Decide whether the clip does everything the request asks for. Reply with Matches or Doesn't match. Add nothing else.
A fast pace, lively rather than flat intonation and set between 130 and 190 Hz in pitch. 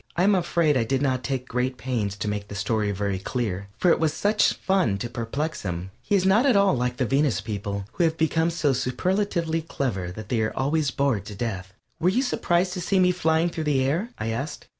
Matches